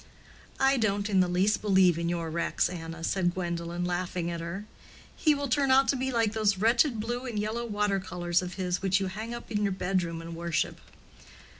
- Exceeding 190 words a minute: Yes, fast, 205 wpm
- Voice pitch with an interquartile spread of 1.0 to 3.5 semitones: No, average, 4.2 semitones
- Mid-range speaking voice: No, high, 195 Hz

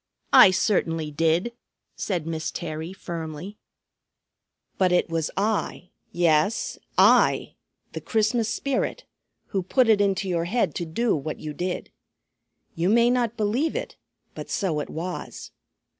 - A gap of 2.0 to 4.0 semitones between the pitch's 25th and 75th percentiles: No, average, 5.0 semitones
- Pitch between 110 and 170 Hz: No, medium, 185 Hz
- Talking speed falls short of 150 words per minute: Yes, slow, 135 wpm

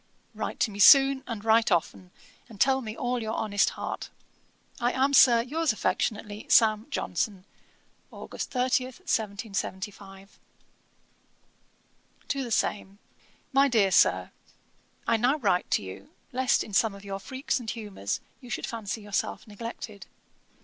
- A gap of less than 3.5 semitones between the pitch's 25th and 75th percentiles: No, average, 3.8 semitones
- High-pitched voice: Yes, high, 220 Hz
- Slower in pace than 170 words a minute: Yes, average, 140 wpm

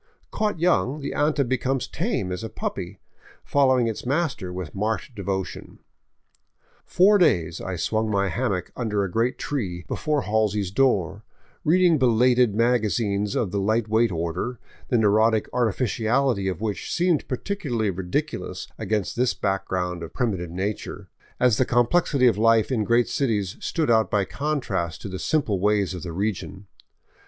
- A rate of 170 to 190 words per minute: No, average, 155 wpm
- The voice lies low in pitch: Yes, low, 110 Hz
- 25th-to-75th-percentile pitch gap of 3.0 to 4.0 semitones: No, average, 4.7 semitones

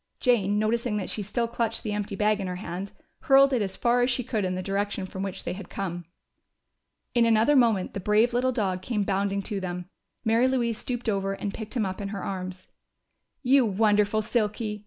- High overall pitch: Yes, high, 210 Hz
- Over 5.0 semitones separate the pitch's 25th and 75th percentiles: No, average, 3.2 semitones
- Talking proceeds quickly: Yes, fast, 210 wpm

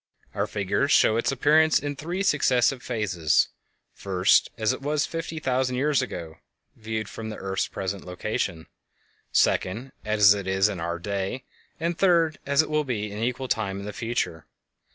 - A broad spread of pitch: Yes, wide, 6.4 semitones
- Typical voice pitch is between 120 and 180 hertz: No, low, 110 Hz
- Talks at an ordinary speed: Yes, average, 170 wpm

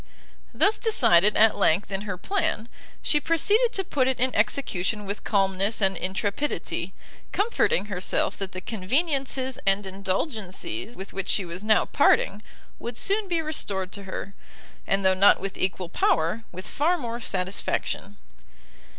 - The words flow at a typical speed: Yes, average, 150 wpm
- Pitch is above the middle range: Yes, high, 205 Hz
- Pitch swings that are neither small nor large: No, wide, 5.7 semitones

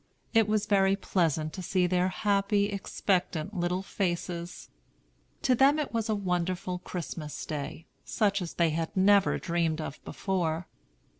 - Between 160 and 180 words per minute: No, average, 145 wpm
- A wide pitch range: No, average, 3.0 semitones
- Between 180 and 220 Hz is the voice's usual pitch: Yes, medium, 185 Hz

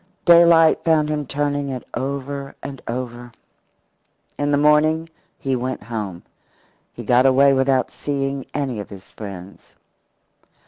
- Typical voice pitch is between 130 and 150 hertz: Yes, low, 135 Hz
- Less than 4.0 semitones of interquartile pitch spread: Yes, average, 3.0 semitones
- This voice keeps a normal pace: No, slow, 130 wpm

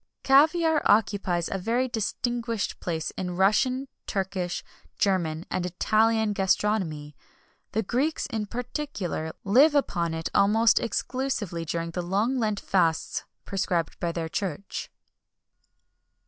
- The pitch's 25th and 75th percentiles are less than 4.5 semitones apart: No, average, 5.2 semitones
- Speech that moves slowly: Yes, slow, 115 wpm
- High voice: Yes, high, 200 Hz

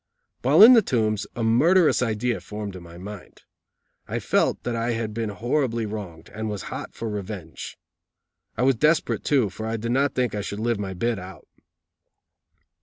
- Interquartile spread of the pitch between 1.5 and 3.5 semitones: Yes, average, 3.1 semitones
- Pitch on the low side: Yes, low, 110 Hz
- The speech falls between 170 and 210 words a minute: Yes, average, 180 wpm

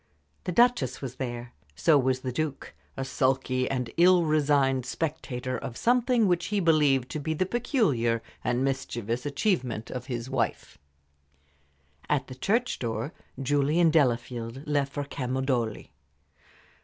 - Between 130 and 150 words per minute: Yes, average, 140 wpm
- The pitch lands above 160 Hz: No, low, 135 Hz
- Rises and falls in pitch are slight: No, average, 3.9 semitones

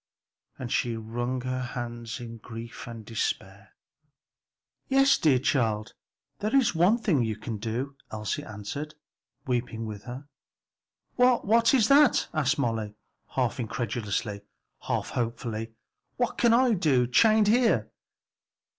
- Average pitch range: No, wide, 7.6 semitones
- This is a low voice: Yes, low, 125 Hz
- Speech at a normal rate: No, slow, 130 wpm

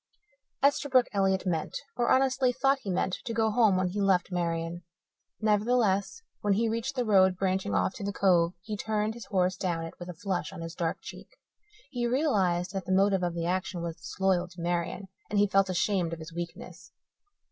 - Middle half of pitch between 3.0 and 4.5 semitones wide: Yes, average, 3.6 semitones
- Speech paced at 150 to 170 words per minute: No, average, 200 wpm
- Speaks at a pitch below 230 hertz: Yes, high, 190 Hz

